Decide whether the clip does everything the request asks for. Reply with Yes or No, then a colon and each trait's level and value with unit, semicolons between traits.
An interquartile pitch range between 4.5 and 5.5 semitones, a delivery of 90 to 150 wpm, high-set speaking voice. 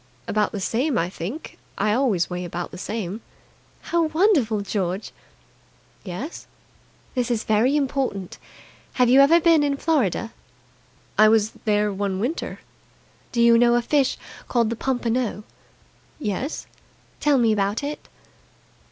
Yes: average, 5.2 semitones; slow, 135 wpm; high, 230 Hz